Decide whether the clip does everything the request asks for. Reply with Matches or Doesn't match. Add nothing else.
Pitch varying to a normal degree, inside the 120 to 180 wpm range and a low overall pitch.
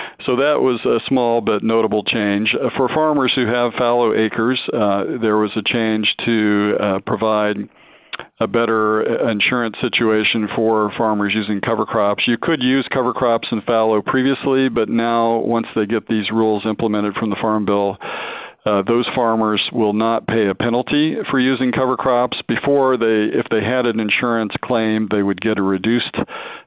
Doesn't match